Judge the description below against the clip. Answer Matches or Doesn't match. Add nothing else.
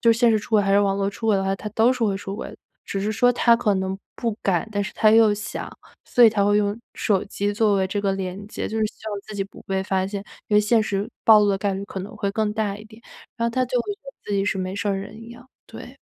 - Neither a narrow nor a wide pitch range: Doesn't match